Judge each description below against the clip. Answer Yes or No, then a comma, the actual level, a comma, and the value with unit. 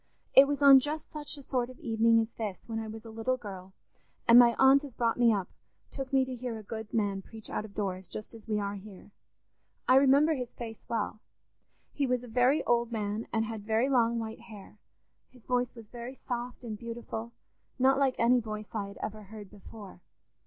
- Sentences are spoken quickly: Yes, fast, 215 wpm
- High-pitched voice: Yes, high, 230 Hz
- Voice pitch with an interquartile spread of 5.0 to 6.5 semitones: No, average, 2.9 semitones